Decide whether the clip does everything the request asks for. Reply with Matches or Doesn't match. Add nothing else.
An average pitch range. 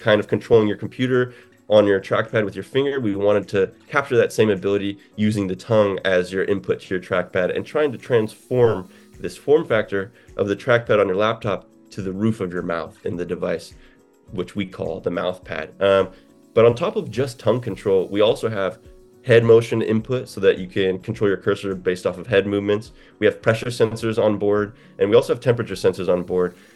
Matches